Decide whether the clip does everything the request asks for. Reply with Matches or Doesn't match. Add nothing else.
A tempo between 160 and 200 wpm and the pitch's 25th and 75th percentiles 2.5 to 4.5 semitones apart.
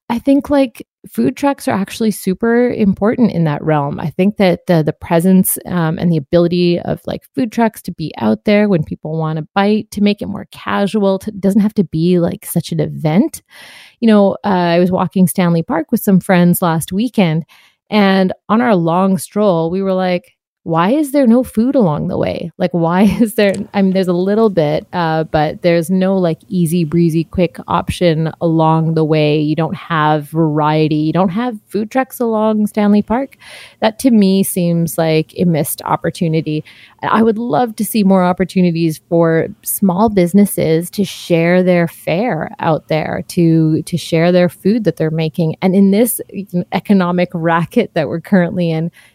Matches